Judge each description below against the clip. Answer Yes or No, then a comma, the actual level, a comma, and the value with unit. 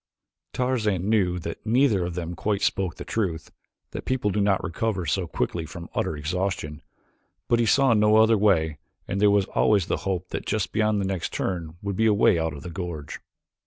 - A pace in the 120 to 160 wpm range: No, average, 200 wpm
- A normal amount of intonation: Yes, average, 4.0 semitones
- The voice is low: Yes, very low, 95 Hz